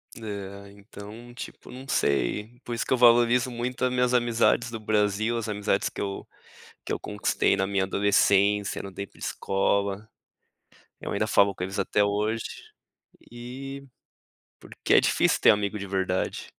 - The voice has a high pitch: No, low, 105 Hz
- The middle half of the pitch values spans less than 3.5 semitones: Yes, average, 3.1 semitones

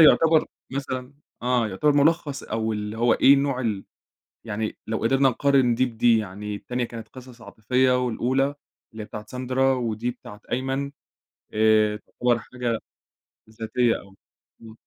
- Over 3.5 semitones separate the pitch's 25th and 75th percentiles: No, average, 3.1 semitones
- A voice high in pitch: No, low, 120 Hz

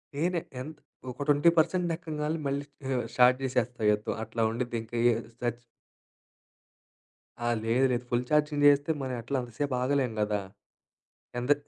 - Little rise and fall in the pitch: No, average, 3.7 semitones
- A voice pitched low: Yes, low, 130 Hz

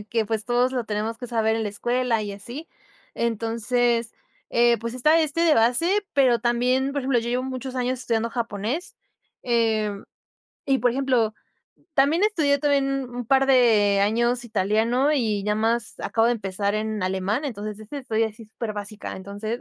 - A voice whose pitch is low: No, high, 235 Hz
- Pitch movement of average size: Yes, average, 3.1 semitones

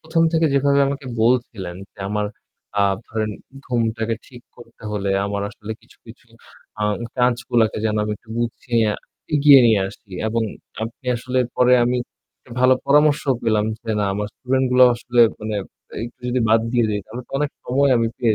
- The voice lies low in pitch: Yes, low, 120 Hz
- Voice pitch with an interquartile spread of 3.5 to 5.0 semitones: No, average, 3.0 semitones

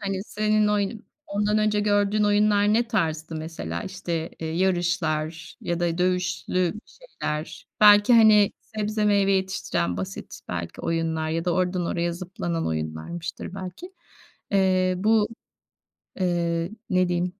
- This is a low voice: No, medium, 185 Hz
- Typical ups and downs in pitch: Yes, average, 3.8 semitones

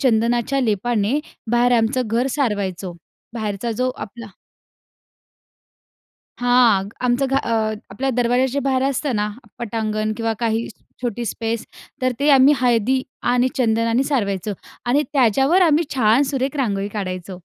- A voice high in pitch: Yes, high, 240 Hz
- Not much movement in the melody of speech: No, average, 3.3 semitones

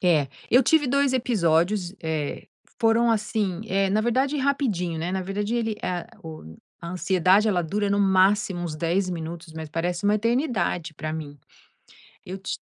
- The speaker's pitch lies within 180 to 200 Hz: Yes, high, 190 Hz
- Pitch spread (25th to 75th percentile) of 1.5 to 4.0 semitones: No, average, 4.7 semitones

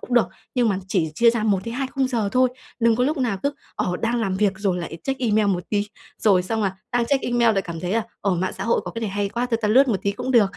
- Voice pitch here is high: Yes, high, 220 Hz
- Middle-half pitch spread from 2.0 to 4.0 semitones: Yes, average, 3.7 semitones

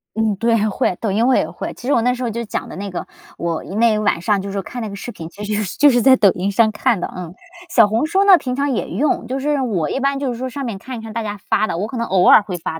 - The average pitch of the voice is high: Yes, high, 220 Hz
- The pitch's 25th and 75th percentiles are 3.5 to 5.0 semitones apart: Yes, average, 4.0 semitones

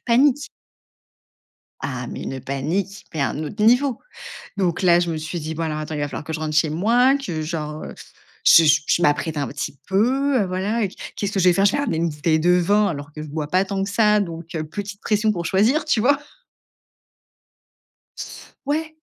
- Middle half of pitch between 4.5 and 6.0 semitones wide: Yes, wide, 5.4 semitones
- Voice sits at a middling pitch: Yes, medium, 180 Hz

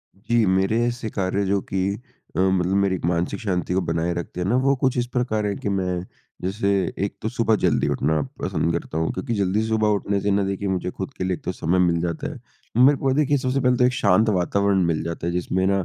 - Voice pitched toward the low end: Yes, very low, 95 Hz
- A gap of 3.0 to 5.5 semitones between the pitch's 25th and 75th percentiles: Yes, average, 3.6 semitones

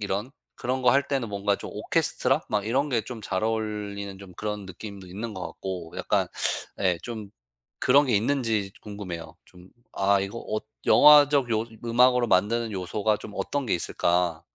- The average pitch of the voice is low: Yes, low, 105 Hz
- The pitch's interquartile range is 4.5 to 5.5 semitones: No, average, 3.8 semitones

